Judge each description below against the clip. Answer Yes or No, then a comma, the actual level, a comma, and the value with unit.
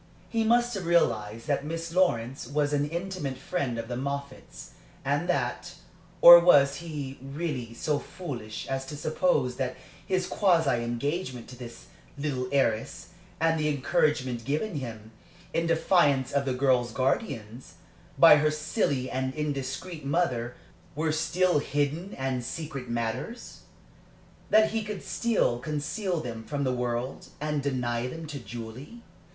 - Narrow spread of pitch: No, average, 4.7 semitones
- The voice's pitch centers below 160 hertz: Yes, medium, 140 Hz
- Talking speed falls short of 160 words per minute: Yes, average, 145 wpm